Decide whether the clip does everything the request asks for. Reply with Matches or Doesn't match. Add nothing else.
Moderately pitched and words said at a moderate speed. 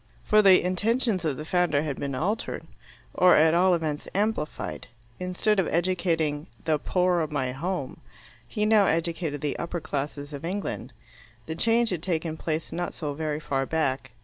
Matches